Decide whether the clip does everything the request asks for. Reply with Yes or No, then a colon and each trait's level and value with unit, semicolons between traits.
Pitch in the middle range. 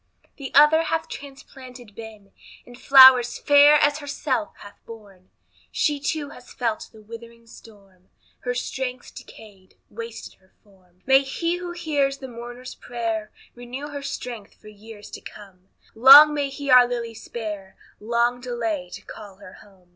No: high, 240 Hz